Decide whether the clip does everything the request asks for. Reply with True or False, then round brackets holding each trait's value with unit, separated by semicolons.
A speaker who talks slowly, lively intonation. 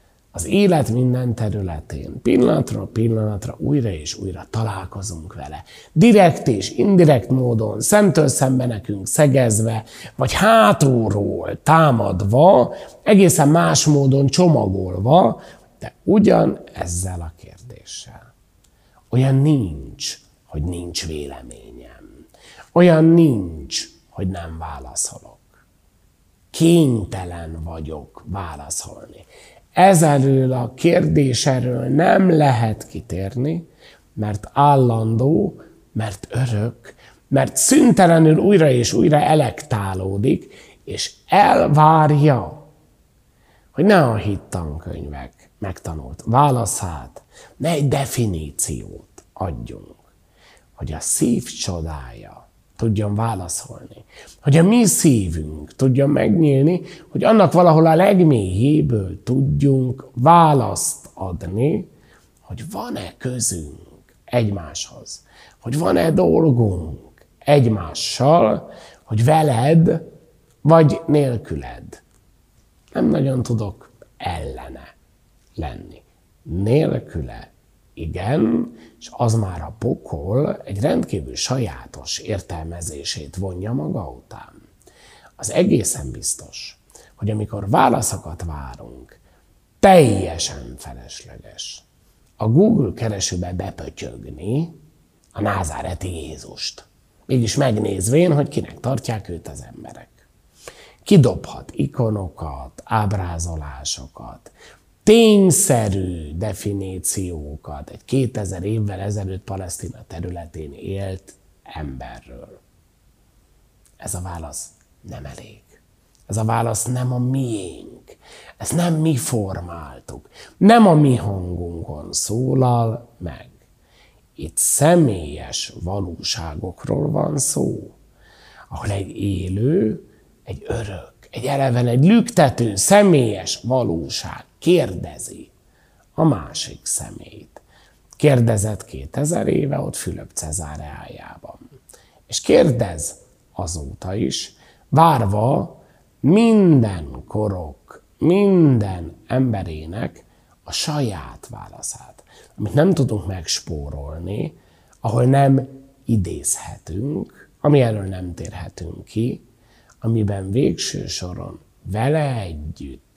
True (90 wpm; 7.6 semitones)